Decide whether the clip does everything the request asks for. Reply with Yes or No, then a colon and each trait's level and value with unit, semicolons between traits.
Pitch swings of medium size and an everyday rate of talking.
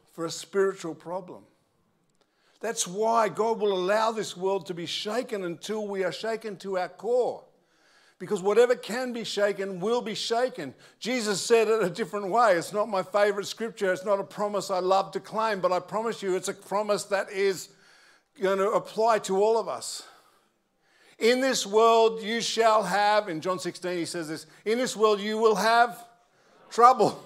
Yes: average, 3.2 semitones; average, 185 wpm